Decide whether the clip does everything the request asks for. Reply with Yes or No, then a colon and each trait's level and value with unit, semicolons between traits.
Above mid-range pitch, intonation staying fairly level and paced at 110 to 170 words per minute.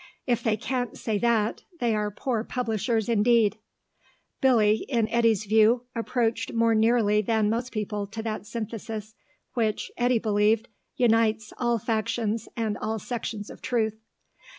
Yes: high, 225 Hz; narrow, 1.7 semitones; average, 140 wpm